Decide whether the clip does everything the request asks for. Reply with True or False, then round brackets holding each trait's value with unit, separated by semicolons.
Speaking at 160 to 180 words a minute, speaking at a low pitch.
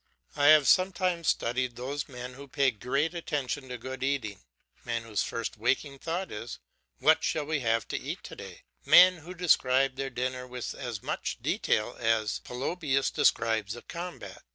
True (170 wpm; 130 Hz)